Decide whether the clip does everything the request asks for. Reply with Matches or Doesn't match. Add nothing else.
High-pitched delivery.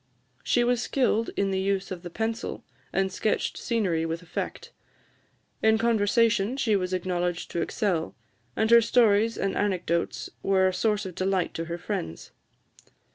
Matches